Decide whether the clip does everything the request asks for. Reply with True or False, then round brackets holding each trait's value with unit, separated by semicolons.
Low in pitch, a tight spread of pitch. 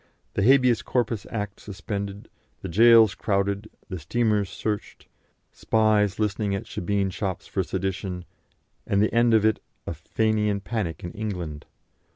True (105 Hz; 2.1 semitones)